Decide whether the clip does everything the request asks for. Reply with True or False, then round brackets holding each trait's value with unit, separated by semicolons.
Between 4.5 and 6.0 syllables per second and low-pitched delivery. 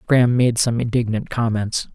True (5.1 syllables/s; 115 Hz)